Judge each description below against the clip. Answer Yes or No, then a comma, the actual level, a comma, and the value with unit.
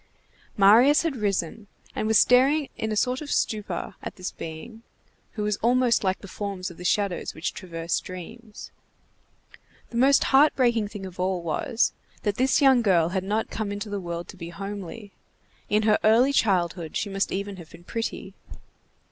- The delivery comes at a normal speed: Yes, average, 180 wpm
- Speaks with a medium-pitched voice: No, high, 205 Hz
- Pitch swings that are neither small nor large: Yes, average, 4.0 semitones